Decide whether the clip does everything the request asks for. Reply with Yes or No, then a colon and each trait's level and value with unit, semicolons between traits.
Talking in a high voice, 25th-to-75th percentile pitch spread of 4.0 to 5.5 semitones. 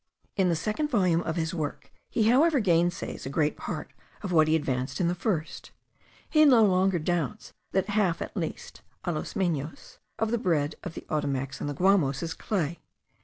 No: medium, 175 Hz; average, 4.5 semitones